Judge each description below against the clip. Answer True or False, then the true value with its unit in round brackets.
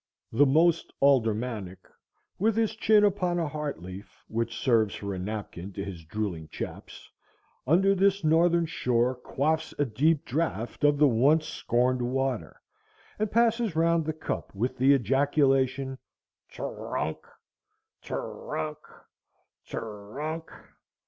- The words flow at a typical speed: True (150 wpm)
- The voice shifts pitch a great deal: True (6.2 semitones)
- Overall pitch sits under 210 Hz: True (135 Hz)